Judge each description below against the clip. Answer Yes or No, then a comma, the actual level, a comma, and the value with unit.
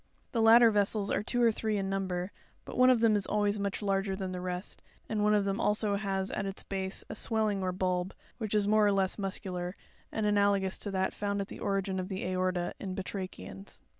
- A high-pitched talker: Yes, high, 195 Hz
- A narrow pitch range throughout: Yes, narrow, 1.8 semitones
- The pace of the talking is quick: Yes, fast, 225 wpm